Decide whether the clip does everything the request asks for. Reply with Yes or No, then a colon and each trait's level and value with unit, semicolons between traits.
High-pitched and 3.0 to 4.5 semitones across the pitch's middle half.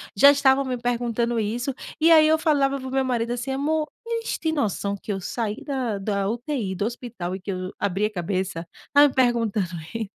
No: high, 240 Hz; average, 5.3 semitones